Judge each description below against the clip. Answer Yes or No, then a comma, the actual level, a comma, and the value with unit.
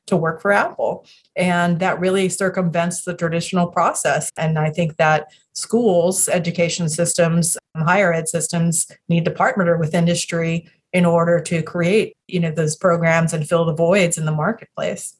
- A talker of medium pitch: Yes, medium, 170 Hz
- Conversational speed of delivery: Yes, average, 160 wpm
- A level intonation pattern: Yes, narrow, 1.3 semitones